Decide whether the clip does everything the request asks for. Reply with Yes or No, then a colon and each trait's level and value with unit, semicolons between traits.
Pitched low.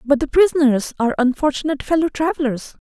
No: very high, 285 Hz